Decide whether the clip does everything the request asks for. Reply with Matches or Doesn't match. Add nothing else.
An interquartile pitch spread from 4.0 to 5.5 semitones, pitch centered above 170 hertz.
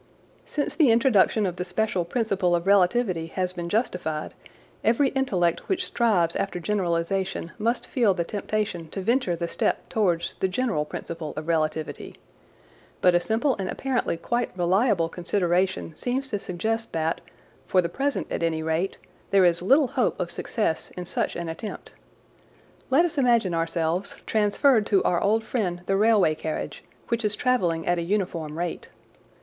Matches